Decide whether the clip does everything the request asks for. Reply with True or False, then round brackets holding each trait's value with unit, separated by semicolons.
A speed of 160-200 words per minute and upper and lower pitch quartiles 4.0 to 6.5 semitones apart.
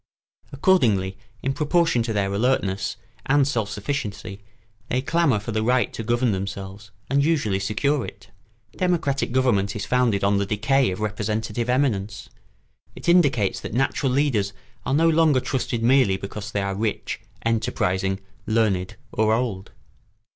False (145 wpm; 5.0 semitones)